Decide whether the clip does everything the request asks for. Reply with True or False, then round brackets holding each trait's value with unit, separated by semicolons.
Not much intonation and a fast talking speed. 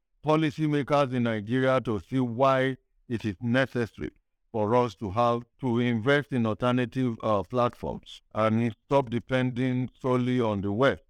False (2.2 semitones; 140 wpm)